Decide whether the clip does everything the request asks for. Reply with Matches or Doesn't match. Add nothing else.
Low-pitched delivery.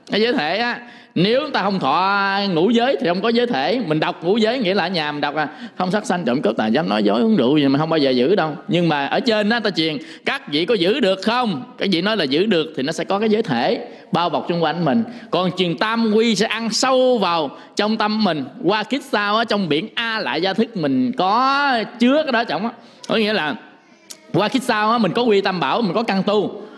Doesn't match